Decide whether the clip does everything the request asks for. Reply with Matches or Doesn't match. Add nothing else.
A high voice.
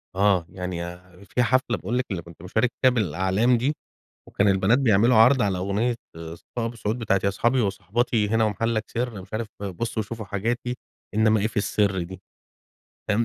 Doesn't match